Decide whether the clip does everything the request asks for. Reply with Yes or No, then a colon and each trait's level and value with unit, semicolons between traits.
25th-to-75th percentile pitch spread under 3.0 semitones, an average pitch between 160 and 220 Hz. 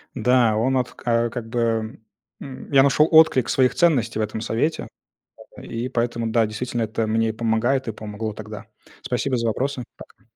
No: narrow, 2.5 semitones; low, 115 Hz